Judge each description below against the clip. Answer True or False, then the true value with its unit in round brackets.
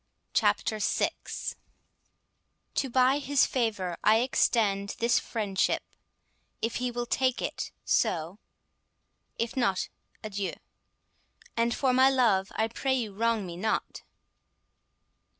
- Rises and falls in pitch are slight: False (3.9 semitones)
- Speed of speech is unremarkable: False (115 wpm)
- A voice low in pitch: False (230 Hz)